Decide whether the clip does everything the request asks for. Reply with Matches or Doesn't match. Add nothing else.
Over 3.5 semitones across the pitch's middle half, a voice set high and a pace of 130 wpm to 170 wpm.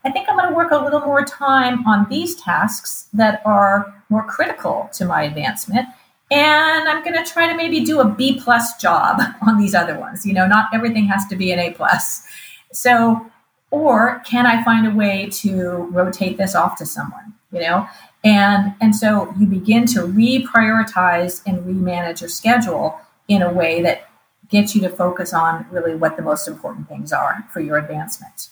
Doesn't match